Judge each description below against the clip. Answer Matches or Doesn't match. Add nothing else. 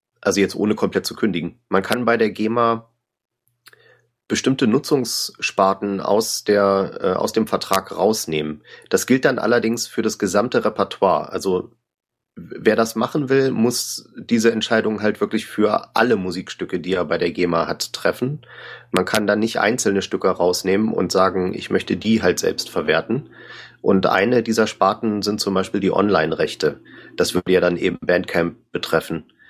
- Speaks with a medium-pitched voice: Doesn't match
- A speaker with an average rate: Matches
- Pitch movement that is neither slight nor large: Matches